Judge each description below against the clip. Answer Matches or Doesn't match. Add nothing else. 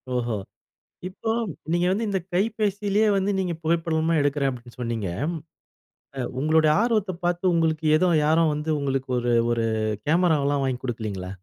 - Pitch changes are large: Matches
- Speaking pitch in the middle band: Matches